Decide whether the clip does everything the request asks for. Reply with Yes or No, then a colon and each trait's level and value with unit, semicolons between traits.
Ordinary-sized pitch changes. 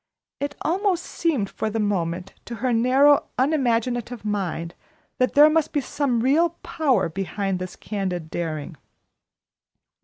No: wide, 6.9 semitones